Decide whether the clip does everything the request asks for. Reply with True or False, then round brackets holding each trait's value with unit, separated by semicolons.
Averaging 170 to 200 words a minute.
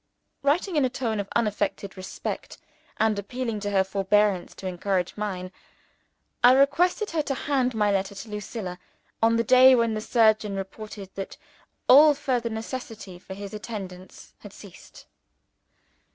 False (150 wpm)